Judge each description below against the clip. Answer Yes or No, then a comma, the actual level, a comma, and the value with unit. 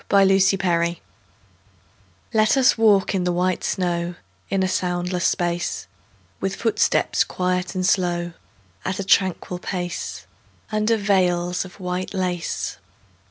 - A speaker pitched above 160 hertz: Yes, medium, 185 Hz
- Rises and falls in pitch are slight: Yes, narrow, 1.6 semitones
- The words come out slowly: Yes, slow, 120 wpm